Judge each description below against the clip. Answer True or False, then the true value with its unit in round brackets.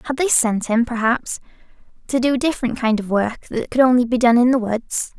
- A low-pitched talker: False (240 Hz)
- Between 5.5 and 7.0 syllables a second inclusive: True (5.6 syllables/s)